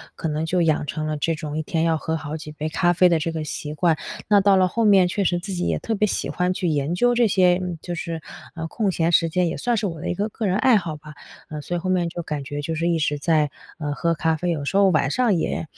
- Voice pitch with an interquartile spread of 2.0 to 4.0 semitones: Yes, average, 3.0 semitones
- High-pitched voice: No, medium, 170 Hz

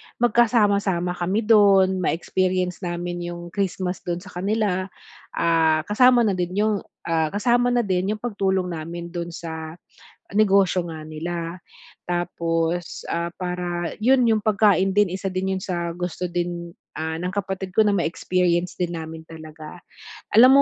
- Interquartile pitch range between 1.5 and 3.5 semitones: Yes, average, 2.8 semitones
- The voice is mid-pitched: Yes, medium, 180 Hz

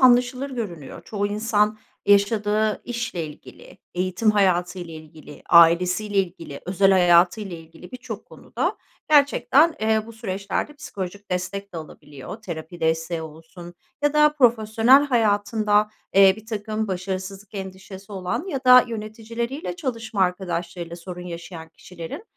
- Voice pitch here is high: Yes, high, 200 Hz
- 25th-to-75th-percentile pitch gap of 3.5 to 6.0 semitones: Yes, average, 4.1 semitones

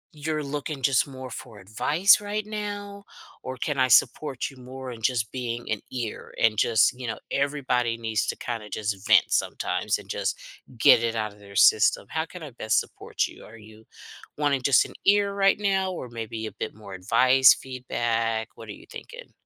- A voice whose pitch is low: Yes, low, 125 Hz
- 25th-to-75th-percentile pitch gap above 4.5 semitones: Yes, average, 4.9 semitones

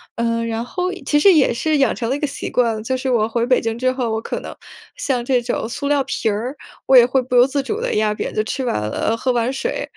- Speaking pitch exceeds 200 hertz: Yes, very high, 250 Hz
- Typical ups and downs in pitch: Yes, average, 3.0 semitones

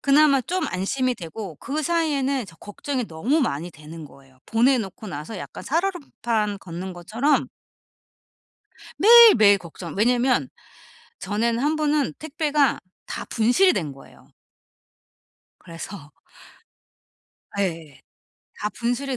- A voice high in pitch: Yes, high, 230 Hz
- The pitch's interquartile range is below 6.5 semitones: No, wide, 7.9 semitones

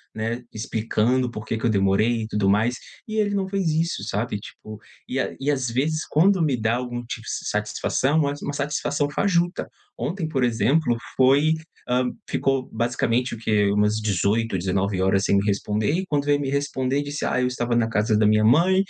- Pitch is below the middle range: Yes, low, 125 Hz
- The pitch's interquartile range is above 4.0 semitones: Yes, average, 5.0 semitones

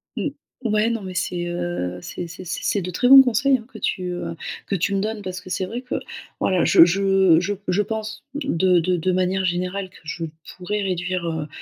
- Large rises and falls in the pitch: No, average, 2.9 semitones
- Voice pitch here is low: No, medium, 185 Hz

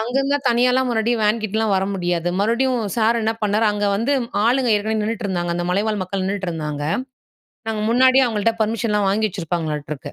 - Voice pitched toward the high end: Yes, high, 215 Hz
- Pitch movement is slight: No, average, 3.7 semitones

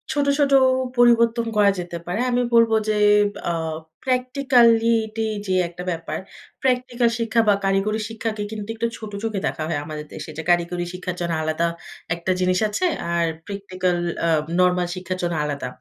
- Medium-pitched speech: No, high, 205 Hz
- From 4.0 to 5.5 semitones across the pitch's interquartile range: Yes, average, 4.7 semitones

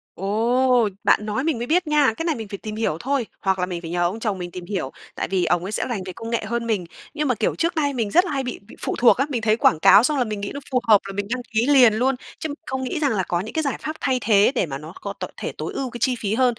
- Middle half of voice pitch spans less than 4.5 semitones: No, average, 4.8 semitones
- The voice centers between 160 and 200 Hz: No, high, 230 Hz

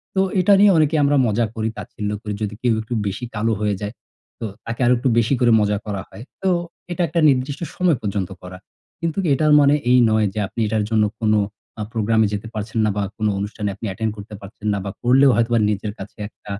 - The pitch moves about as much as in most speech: Yes, average, 3.4 semitones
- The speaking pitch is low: Yes, low, 110 Hz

